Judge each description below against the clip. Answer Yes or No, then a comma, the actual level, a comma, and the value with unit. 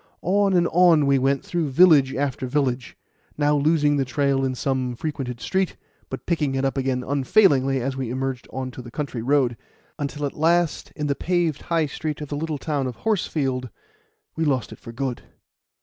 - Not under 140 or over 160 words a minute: No, average, 190 wpm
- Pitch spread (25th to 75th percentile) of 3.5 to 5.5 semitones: No, average, 3.0 semitones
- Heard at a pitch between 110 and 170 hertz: Yes, medium, 140 Hz